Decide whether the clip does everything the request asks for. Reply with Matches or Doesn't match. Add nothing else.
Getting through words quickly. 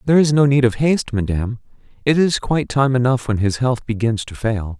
Matches